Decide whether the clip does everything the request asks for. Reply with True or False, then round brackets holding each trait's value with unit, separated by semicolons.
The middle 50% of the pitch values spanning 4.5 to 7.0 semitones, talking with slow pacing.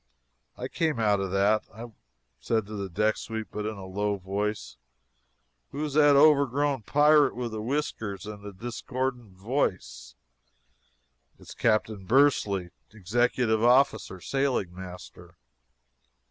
True (4.9 semitones; 130 wpm)